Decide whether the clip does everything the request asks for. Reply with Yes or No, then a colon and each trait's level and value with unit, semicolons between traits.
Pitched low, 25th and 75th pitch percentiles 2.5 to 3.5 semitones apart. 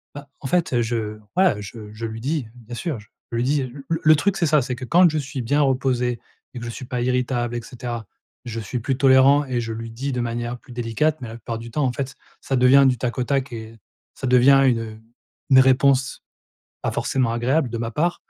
Yes: low, 125 Hz; average, 2.8 semitones